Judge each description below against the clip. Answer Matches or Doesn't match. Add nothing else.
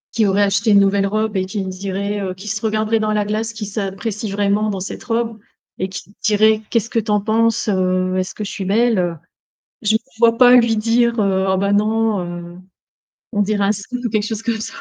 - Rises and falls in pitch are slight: Matches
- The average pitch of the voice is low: Doesn't match